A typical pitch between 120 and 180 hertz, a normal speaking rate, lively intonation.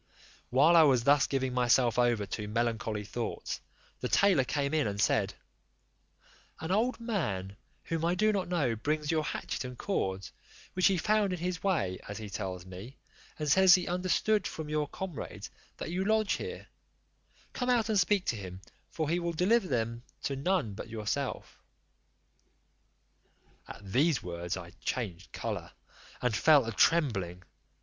Yes: medium, 140 Hz; average, 160 wpm; wide, 8.6 semitones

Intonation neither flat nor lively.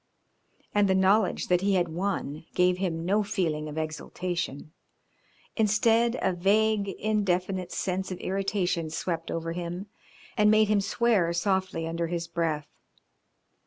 Yes: average, 3.1 semitones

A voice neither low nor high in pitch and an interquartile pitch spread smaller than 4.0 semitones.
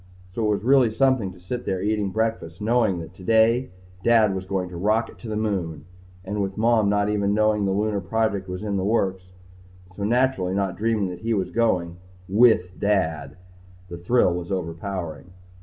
No: low, 100 Hz; average, 3.4 semitones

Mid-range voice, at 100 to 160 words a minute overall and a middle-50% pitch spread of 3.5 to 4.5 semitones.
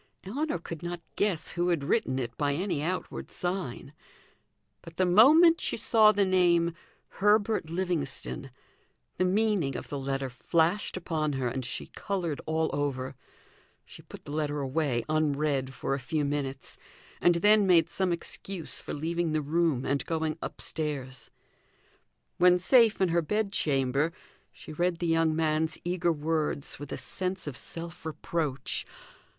Yes: medium, 160 Hz; average, 155 wpm; average, 4.1 semitones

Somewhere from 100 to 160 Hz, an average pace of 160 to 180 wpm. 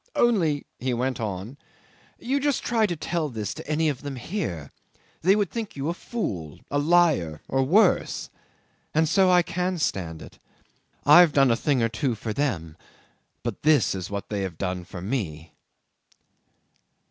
Yes: medium, 140 Hz; average, 170 wpm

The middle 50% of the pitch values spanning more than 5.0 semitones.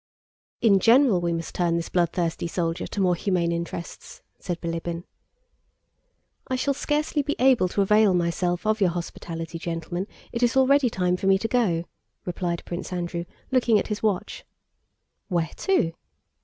No: average, 4.6 semitones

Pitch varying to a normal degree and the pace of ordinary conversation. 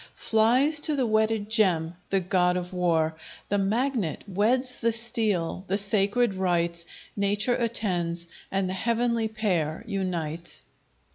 No: average, 4.3 semitones; slow, 130 wpm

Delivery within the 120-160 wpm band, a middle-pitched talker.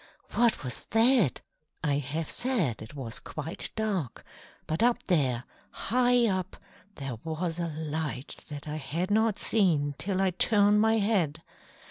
Yes: average, 145 wpm; medium, 170 Hz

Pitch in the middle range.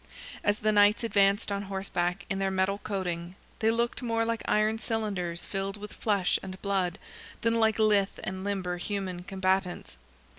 No: high, 200 Hz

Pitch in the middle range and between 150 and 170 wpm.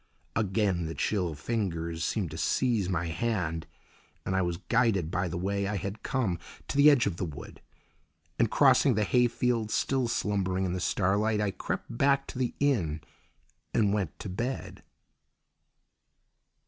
No: low, 100 Hz; average, 160 wpm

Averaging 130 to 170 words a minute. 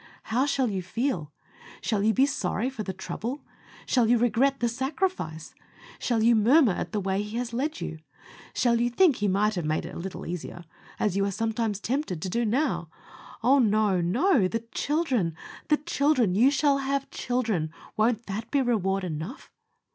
No: average, 185 wpm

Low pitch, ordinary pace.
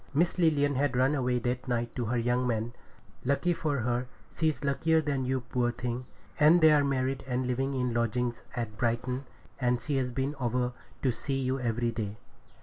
Yes: low, 125 Hz; average, 180 wpm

